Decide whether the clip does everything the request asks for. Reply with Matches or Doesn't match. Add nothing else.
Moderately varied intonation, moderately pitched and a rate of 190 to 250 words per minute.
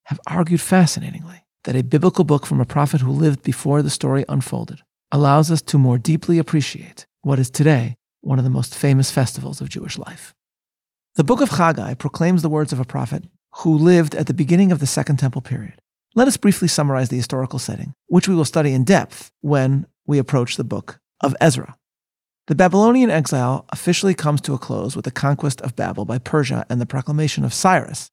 Matches